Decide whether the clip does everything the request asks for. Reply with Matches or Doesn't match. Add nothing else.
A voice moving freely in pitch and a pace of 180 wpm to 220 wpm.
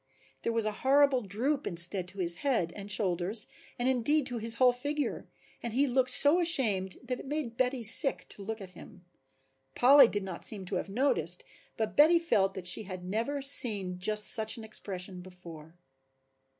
Matches